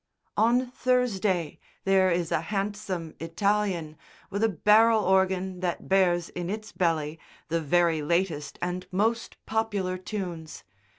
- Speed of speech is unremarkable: No, slow, 125 wpm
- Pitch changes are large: No, average, 3.7 semitones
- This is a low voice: No, medium, 185 Hz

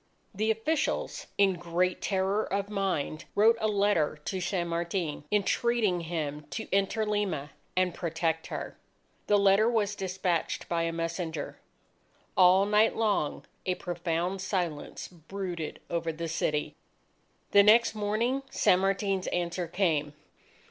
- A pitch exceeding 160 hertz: Yes, medium, 185 Hz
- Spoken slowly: Yes, slow, 130 wpm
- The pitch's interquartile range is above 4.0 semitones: No, average, 3.5 semitones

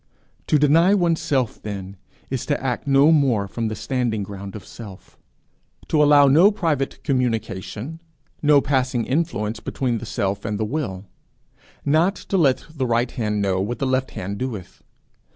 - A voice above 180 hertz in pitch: No, low, 130 Hz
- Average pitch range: No, wide, 5.7 semitones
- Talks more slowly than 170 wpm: Yes, average, 160 wpm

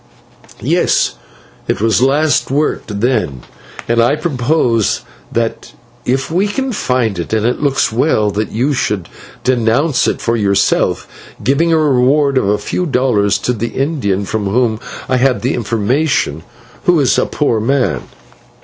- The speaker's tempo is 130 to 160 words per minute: Yes, average, 150 wpm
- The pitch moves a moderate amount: Yes, average, 4.5 semitones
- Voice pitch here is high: No, low, 125 Hz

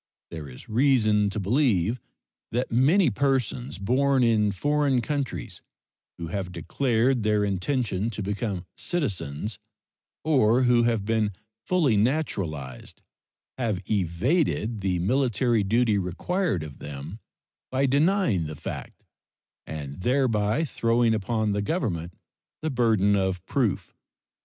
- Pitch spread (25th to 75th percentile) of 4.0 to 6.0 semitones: Yes, average, 5.3 semitones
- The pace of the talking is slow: Yes, slow, 120 wpm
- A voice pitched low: Yes, low, 110 Hz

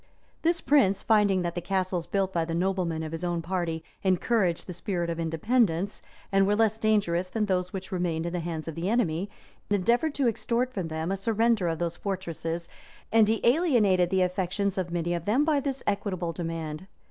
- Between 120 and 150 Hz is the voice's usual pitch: No, medium, 185 Hz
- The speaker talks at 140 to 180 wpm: No, average, 200 wpm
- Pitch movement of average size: Yes, average, 3.9 semitones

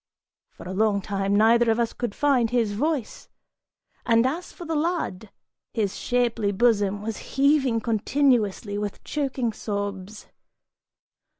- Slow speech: Yes, slow, 130 wpm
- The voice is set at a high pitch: Yes, high, 225 Hz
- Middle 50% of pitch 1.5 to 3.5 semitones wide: No, average, 4.1 semitones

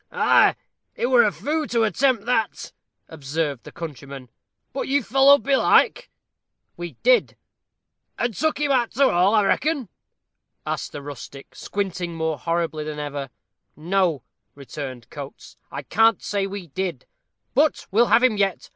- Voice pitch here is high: Yes, high, 195 Hz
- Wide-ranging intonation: Yes, wide, 8.4 semitones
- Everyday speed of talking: Yes, average, 145 wpm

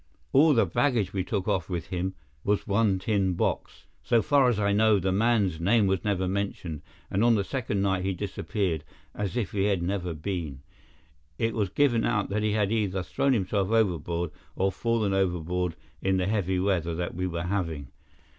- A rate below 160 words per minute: No, average, 190 wpm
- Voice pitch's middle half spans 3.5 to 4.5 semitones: No, average, 2.9 semitones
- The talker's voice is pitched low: Yes, very low, 95 Hz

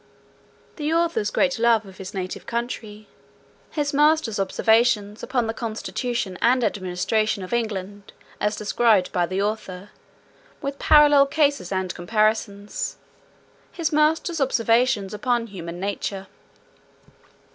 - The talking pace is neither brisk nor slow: No, slow, 115 wpm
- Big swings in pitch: No, average, 4.5 semitones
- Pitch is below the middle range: No, high, 220 Hz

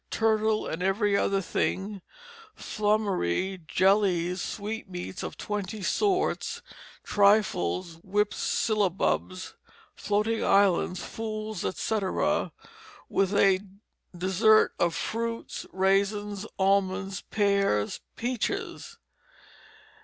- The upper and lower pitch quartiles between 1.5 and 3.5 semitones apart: Yes, narrow, 2.4 semitones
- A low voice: No, high, 200 Hz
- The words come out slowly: Yes, slow, 80 wpm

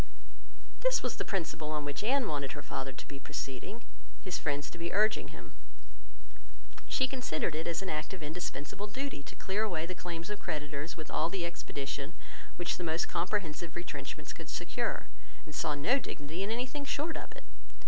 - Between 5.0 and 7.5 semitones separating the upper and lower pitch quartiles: Yes, wide, 5.6 semitones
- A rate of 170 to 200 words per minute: Yes, average, 185 wpm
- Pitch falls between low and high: Yes, medium, 170 Hz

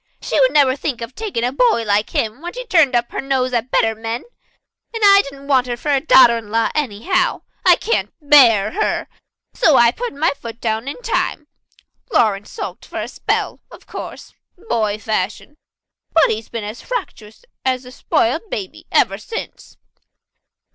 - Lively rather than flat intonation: Yes, wide, 5.8 semitones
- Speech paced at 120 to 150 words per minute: No, average, 180 wpm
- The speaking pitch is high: Yes, very high, 255 Hz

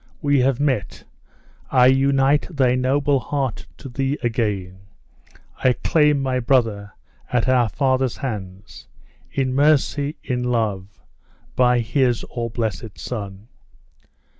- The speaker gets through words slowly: Yes, slow, 115 wpm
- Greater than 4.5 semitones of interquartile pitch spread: No, average, 3.3 semitones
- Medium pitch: No, low, 125 Hz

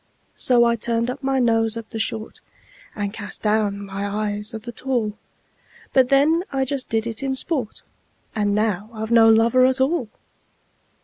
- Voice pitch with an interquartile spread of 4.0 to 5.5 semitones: No, average, 3.2 semitones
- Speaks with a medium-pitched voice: No, high, 225 Hz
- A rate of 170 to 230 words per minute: Yes, average, 175 wpm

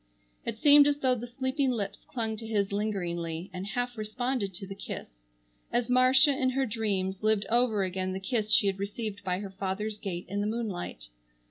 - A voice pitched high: Yes, high, 210 Hz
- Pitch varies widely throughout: No, average, 4.1 semitones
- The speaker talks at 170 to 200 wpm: Yes, average, 195 wpm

